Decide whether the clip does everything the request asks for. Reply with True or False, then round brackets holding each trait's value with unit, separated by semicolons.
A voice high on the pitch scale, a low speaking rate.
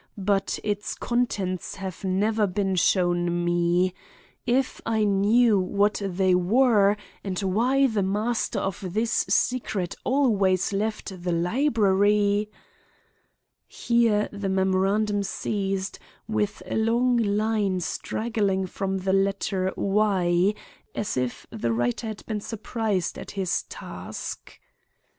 True (200 Hz; 115 wpm)